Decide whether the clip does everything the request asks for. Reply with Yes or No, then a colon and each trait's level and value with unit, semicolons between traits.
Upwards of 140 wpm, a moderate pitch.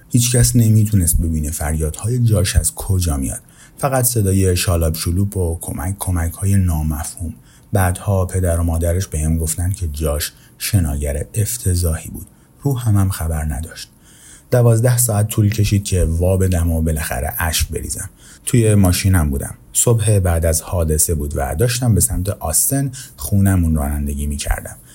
No: average, 150 wpm; very low, 90 Hz